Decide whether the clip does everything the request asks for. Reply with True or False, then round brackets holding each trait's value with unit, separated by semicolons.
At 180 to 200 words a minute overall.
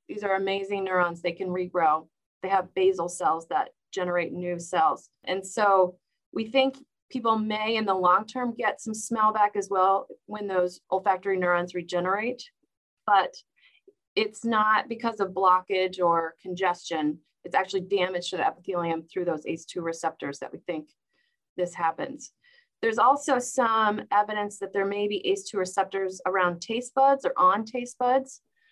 False (160 wpm)